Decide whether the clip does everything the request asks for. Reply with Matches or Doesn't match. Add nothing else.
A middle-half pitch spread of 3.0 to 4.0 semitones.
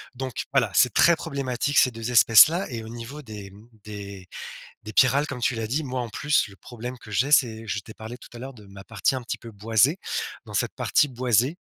Matches